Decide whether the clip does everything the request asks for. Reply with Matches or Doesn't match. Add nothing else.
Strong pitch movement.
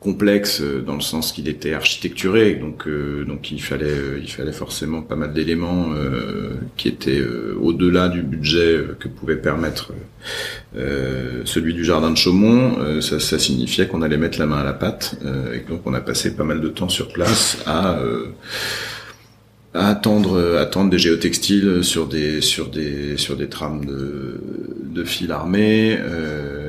Doesn't match